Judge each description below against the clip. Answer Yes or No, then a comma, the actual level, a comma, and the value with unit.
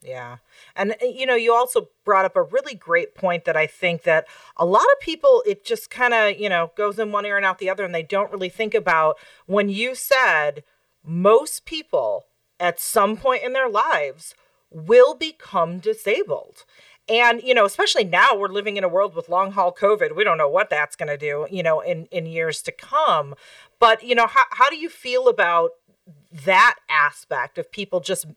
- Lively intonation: Yes, wide, 6.6 semitones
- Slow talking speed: No, fast, 205 wpm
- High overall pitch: Yes, high, 205 Hz